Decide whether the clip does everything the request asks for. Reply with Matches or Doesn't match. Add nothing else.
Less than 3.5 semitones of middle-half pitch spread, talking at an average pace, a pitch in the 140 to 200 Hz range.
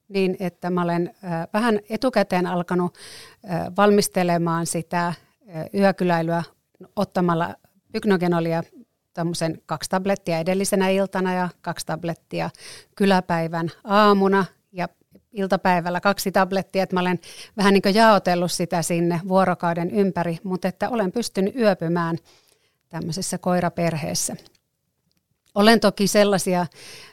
Matches